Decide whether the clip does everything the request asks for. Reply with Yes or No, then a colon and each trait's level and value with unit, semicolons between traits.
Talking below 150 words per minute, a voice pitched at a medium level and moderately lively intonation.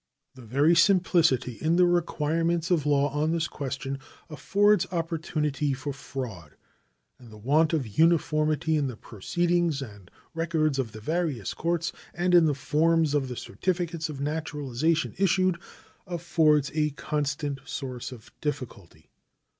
Yes: average, 140 wpm; medium, 150 Hz; average, 3.7 semitones